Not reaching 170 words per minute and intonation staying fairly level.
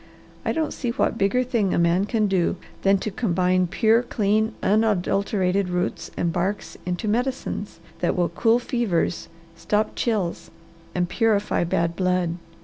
No: average, 145 wpm; average, 3.8 semitones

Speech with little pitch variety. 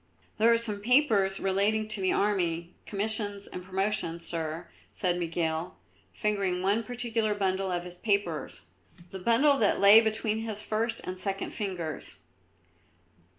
No: average, 3.2 semitones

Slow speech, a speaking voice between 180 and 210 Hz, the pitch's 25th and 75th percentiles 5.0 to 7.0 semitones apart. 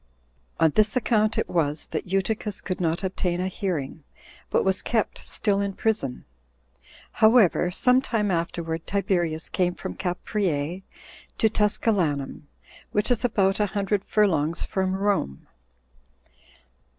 No: slow, 125 wpm; high, 190 Hz; average, 3.7 semitones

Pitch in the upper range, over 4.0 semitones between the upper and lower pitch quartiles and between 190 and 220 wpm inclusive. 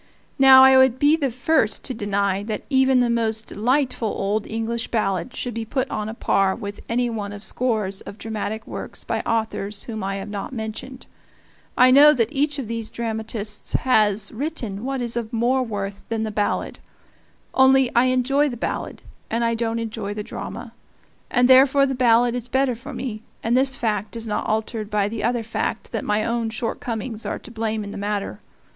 No: high, 230 Hz; average, 3.1 semitones; average, 195 wpm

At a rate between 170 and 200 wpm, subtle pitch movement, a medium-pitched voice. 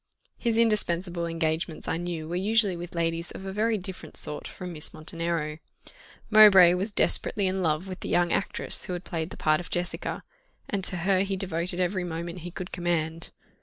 Yes: average, 190 wpm; narrow, 2.3 semitones; medium, 175 Hz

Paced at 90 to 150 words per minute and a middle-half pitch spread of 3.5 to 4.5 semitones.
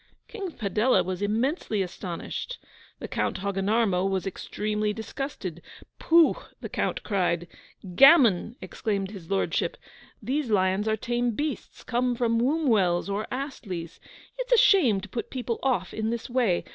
No: average, 145 wpm; average, 4.9 semitones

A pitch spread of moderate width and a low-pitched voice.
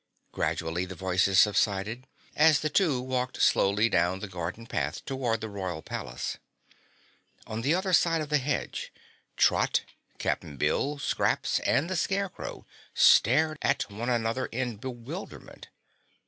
No: wide, 7.1 semitones; low, 120 Hz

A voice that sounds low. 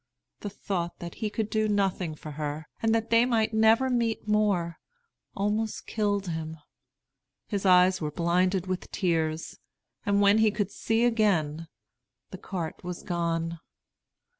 No: high, 195 Hz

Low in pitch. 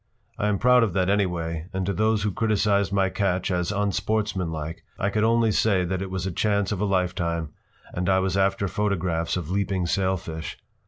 Yes: very low, 95 Hz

